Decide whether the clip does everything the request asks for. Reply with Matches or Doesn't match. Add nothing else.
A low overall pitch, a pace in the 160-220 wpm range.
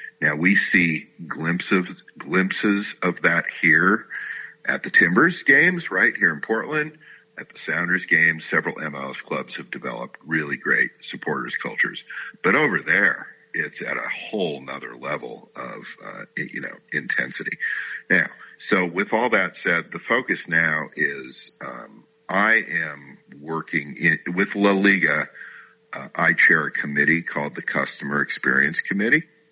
Doesn't match